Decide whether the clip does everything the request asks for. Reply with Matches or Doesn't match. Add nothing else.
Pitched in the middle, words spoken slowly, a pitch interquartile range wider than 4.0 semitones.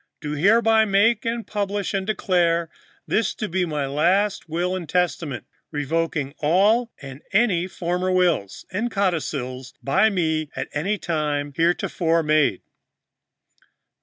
Matches